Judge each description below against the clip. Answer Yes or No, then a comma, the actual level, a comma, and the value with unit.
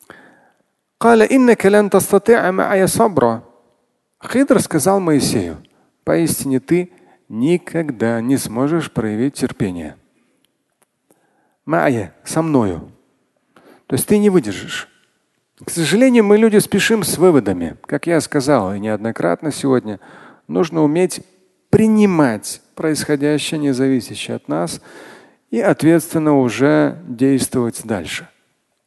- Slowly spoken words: Yes, slow, 100 wpm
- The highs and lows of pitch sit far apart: Yes, wide, 7.0 semitones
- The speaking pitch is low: No, medium, 155 Hz